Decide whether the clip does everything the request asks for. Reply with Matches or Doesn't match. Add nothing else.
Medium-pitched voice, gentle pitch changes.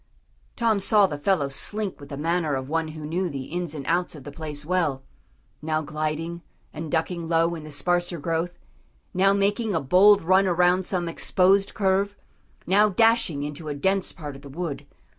Doesn't match